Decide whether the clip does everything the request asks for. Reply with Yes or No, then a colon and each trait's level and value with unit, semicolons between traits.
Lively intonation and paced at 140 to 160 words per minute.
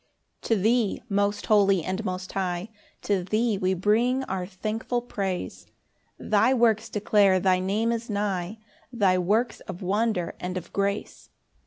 No: average, 3.1 semitones; average, 150 wpm